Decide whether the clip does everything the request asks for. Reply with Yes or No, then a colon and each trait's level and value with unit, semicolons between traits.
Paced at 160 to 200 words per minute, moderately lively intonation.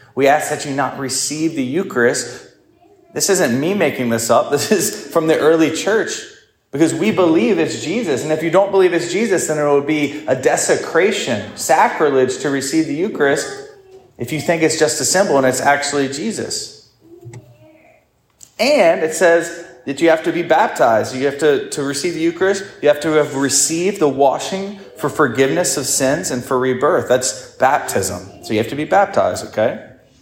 Yes: average, 185 wpm; average, 4.7 semitones